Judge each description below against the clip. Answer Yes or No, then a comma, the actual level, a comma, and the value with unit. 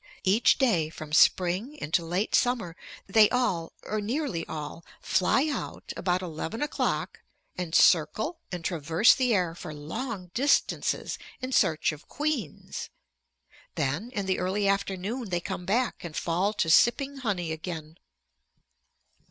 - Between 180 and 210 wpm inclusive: No, slow, 135 wpm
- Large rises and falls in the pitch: Yes, wide, 6.4 semitones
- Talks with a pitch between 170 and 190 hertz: Yes, medium, 185 Hz